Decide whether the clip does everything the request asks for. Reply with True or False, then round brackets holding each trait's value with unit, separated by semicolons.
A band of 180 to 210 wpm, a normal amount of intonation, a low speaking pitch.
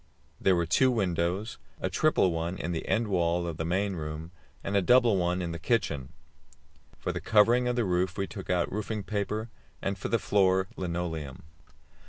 True (190 wpm; 3.6 semitones; 95 Hz)